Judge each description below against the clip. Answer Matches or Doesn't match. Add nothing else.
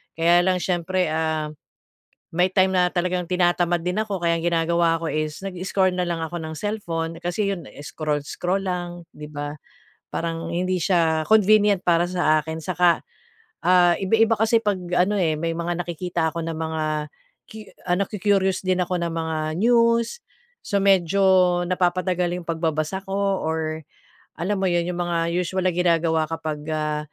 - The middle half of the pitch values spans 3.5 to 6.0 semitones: Doesn't match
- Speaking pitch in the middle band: Matches